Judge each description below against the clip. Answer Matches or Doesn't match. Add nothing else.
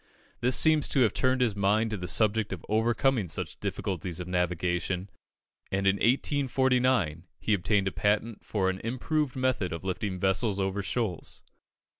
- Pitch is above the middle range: Doesn't match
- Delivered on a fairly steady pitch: Doesn't match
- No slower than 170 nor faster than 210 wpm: Doesn't match